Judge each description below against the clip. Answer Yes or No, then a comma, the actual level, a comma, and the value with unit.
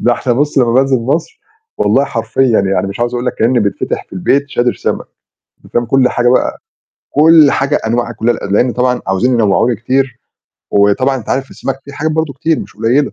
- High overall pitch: No, low, 125 Hz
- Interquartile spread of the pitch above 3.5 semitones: No, average, 2.9 semitones